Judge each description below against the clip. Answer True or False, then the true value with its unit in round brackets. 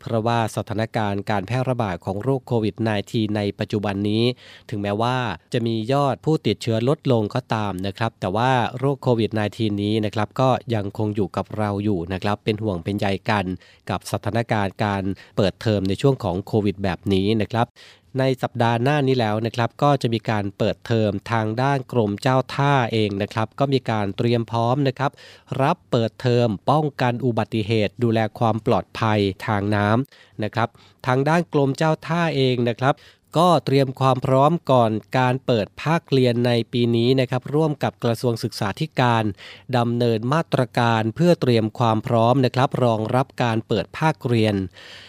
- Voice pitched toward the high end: False (115 Hz)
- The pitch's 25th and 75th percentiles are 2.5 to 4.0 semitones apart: True (3.6 semitones)